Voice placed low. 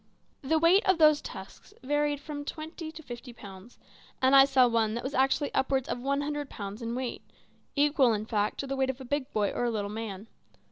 No: very high, 265 Hz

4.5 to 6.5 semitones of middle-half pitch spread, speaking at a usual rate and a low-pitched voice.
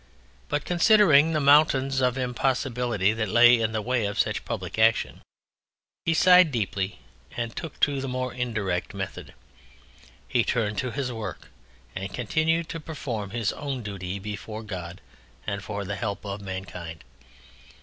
Yes: average, 5.1 semitones; average, 150 wpm; low, 115 Hz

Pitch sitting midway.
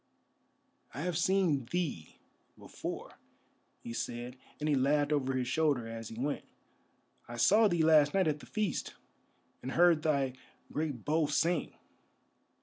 Yes: medium, 150 Hz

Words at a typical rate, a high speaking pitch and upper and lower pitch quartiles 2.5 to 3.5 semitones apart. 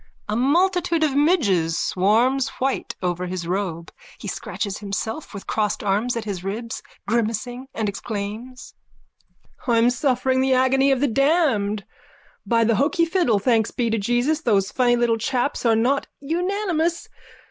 No: average, 145 wpm; high, 240 Hz; average, 4.8 semitones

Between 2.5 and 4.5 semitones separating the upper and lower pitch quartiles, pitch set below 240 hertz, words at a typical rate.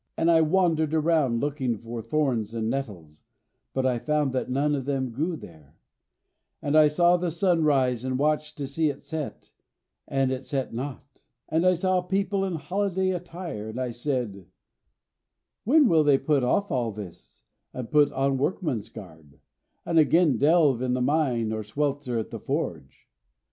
No: average, 4.9 semitones; medium, 140 Hz; average, 170 wpm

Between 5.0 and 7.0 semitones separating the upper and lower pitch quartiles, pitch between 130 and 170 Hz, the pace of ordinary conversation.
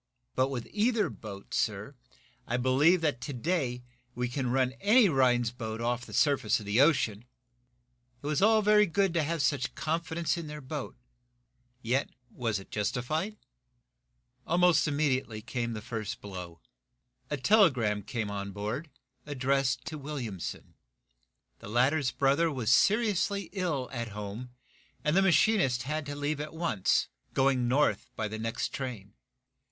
Yes: wide, 5.4 semitones; low, 135 Hz; average, 155 wpm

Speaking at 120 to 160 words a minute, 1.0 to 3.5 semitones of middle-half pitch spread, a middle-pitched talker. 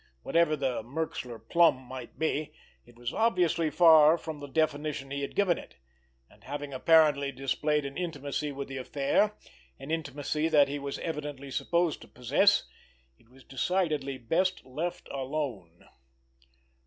Yes: average, 145 wpm; average, 3.1 semitones; medium, 145 Hz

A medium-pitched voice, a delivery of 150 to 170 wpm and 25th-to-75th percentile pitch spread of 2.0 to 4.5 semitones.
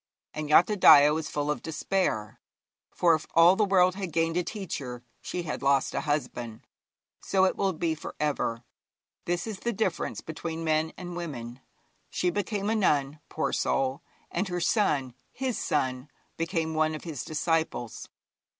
Yes: medium, 160 Hz; average, 160 wpm; average, 3.7 semitones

